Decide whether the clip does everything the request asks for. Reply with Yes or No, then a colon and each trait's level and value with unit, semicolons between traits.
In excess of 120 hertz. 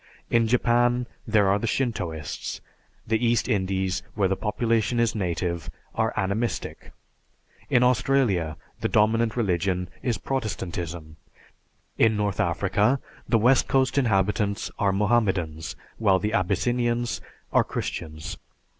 No: low, 105 Hz